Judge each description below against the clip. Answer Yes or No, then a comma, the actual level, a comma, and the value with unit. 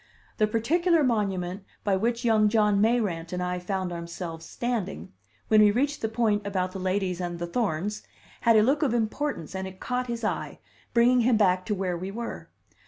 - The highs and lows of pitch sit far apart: No, average, 4.3 semitones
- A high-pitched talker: Yes, high, 210 Hz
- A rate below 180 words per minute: No, average, 190 wpm